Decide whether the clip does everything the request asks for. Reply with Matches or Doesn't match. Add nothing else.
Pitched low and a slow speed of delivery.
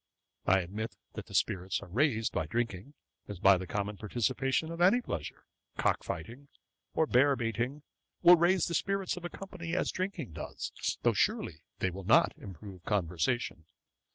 Doesn't match